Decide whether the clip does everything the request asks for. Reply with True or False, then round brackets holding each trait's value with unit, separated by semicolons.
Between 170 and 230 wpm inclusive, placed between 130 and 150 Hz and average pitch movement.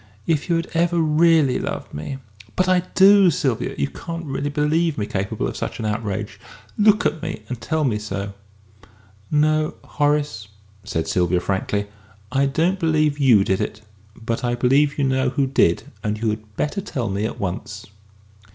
False (180 wpm; 135 Hz; 6.9 semitones)